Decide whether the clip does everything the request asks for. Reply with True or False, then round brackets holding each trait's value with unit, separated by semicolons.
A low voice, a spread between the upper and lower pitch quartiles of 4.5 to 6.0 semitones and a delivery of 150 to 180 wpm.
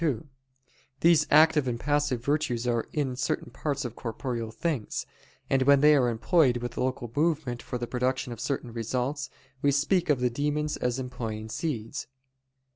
False (130 Hz; 3.5 semitones; 165 wpm)